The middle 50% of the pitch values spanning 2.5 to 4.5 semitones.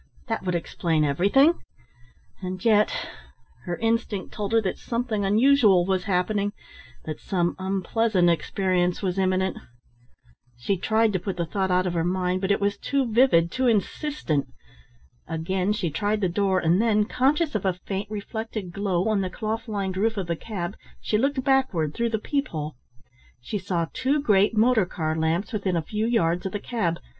Yes: average, 3.7 semitones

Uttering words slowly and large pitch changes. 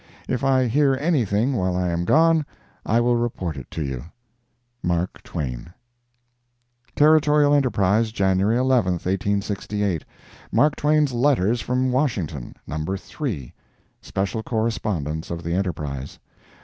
Yes: slow, 120 wpm; wide, 6.7 semitones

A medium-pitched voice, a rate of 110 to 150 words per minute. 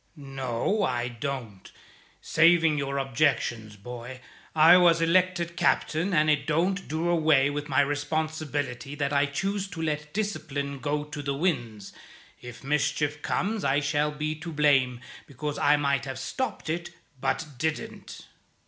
Yes: medium, 150 Hz; average, 145 wpm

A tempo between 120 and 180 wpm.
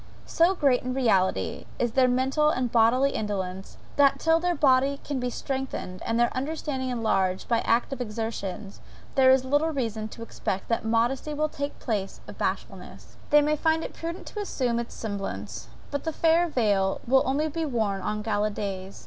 Yes: average, 175 wpm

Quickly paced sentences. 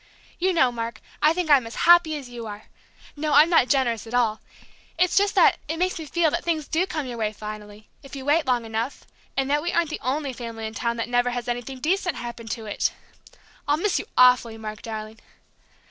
Yes: fast, 225 wpm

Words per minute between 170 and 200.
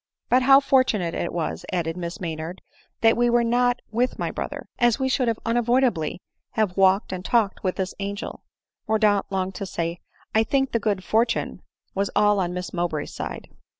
Yes: average, 190 wpm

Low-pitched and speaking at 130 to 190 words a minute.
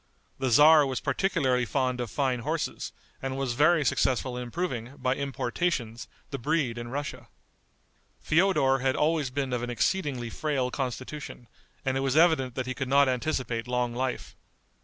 Yes: low, 130 Hz; average, 160 wpm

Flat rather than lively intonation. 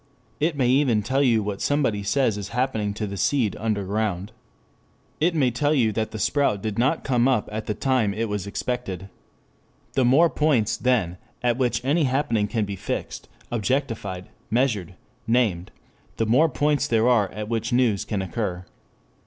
No: average, 4.1 semitones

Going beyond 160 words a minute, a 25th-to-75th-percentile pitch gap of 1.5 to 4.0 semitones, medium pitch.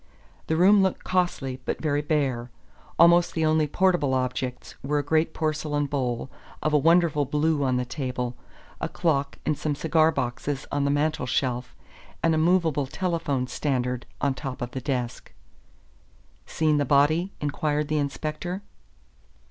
No: average, 155 wpm; average, 3.3 semitones; medium, 145 Hz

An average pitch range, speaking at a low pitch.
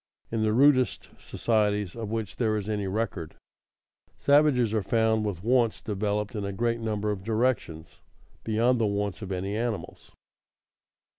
No: narrow, 2.2 semitones; low, 110 Hz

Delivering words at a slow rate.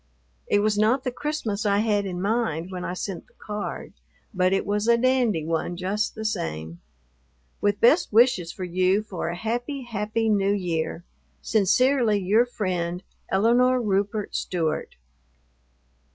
No: average, 150 wpm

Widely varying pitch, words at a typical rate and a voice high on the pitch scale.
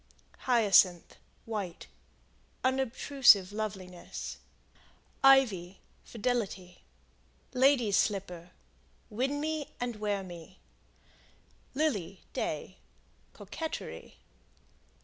No: wide, 5.8 semitones; slow, 65 wpm; high, 210 Hz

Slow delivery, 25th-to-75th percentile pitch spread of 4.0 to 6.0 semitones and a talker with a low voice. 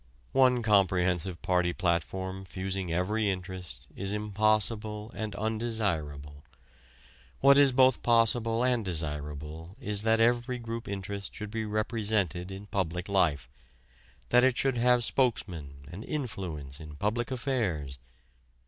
Yes: slow, 120 wpm; average, 4.6 semitones; low, 100 Hz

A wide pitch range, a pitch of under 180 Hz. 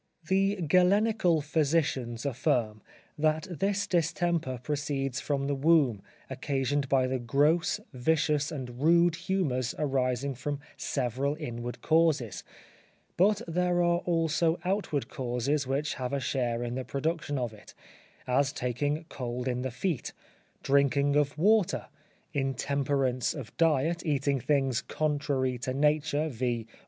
No: average, 4.0 semitones; medium, 140 Hz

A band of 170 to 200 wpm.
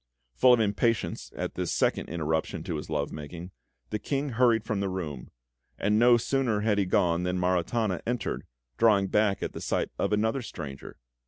Yes: average, 180 wpm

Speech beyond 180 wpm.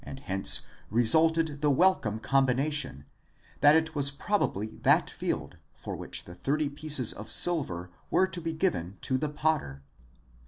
No: average, 150 wpm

